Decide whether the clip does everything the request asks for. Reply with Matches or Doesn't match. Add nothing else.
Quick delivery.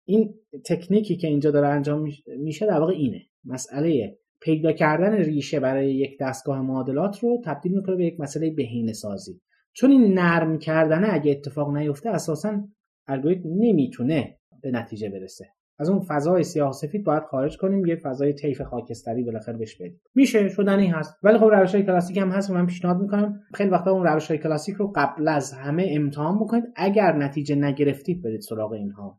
Matches